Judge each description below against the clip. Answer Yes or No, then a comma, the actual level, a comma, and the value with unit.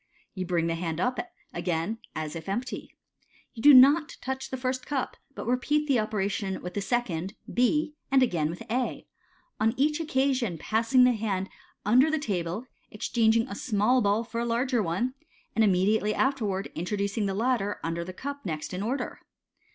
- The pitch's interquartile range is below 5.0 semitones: No, average, 5.3 semitones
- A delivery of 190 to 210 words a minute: No, average, 175 wpm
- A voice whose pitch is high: Yes, high, 220 Hz